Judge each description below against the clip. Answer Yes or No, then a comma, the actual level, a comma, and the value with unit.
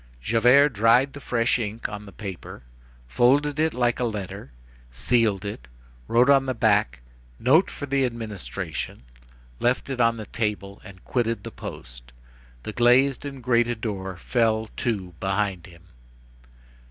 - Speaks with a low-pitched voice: Yes, low, 115 Hz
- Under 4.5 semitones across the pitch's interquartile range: Yes, average, 4.0 semitones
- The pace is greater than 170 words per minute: No, average, 145 wpm